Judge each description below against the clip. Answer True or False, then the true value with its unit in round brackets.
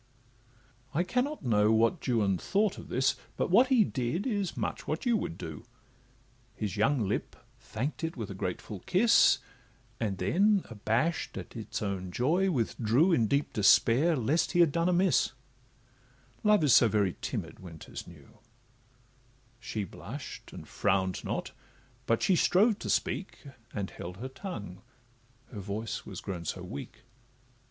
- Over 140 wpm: True (155 wpm)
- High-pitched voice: False (120 Hz)